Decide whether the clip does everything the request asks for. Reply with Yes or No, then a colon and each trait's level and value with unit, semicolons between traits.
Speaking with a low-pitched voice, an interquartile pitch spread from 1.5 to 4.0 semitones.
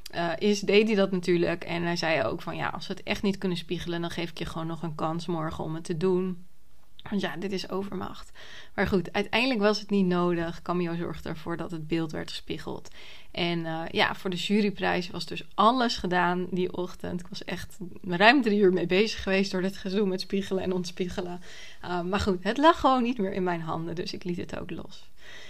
No: medium, 185 Hz; narrow, 2.4 semitones